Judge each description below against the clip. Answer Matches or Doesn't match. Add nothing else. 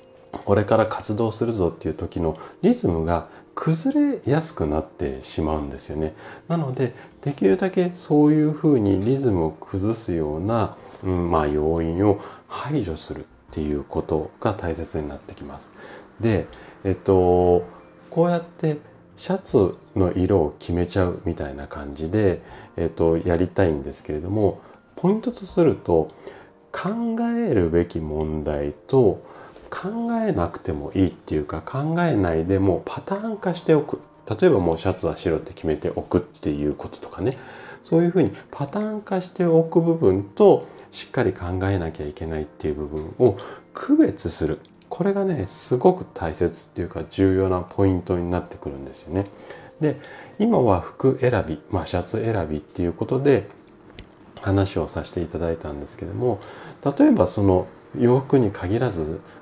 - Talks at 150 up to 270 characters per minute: Doesn't match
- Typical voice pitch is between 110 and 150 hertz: Doesn't match